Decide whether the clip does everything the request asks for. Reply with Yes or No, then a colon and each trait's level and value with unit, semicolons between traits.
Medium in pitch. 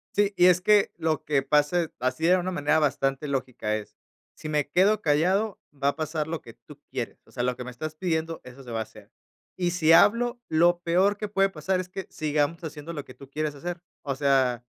Yes: medium, 155 Hz